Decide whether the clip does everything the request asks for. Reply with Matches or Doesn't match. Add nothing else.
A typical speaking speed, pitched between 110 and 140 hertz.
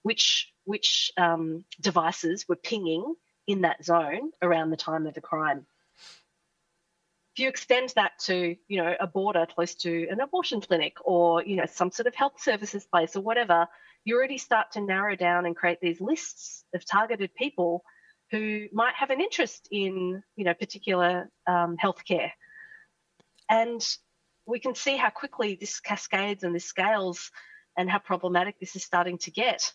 Doesn't match